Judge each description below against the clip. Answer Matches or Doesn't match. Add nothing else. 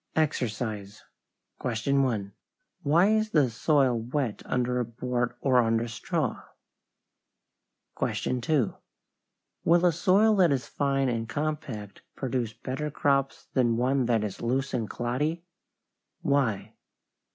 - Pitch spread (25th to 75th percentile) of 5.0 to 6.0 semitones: Doesn't match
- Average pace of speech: Doesn't match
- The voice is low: Matches